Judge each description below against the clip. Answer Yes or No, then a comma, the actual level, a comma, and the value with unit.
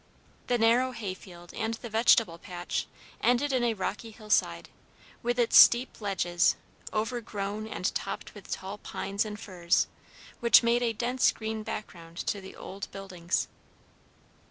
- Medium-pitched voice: No, high, 215 Hz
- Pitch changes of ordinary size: Yes, average, 3.7 semitones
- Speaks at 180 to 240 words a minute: No, average, 145 wpm